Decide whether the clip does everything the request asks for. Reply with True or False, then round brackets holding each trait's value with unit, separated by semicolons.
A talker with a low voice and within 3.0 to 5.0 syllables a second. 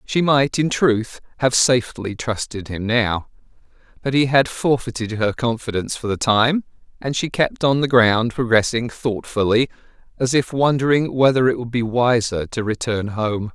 True (120 Hz; 4.6 syllables/s)